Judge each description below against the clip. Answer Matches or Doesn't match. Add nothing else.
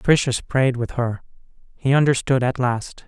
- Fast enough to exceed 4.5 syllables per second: Matches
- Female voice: Doesn't match